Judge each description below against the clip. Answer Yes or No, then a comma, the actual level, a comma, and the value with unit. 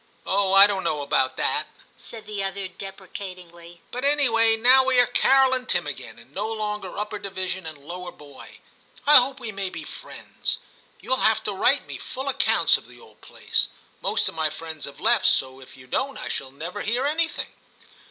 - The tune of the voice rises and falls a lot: Yes, wide, 6.2 semitones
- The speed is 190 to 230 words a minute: Yes, average, 200 wpm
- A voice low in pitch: No, high, 200 Hz